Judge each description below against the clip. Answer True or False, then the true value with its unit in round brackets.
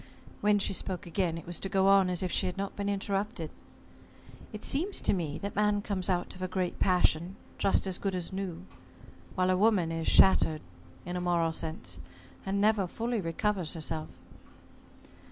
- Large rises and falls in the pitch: False (2.7 semitones)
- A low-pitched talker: False (185 Hz)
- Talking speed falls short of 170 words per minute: False (185 wpm)